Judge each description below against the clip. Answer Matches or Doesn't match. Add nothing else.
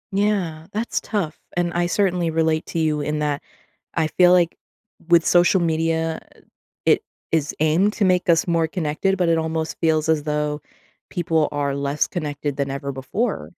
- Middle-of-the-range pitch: Matches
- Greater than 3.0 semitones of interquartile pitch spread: Doesn't match